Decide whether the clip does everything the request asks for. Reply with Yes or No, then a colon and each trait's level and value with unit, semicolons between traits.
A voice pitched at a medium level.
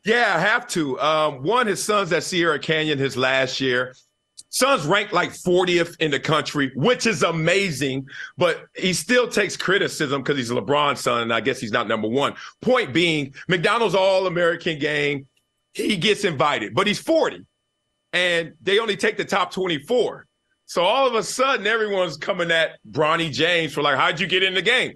Yes: medium, 170 Hz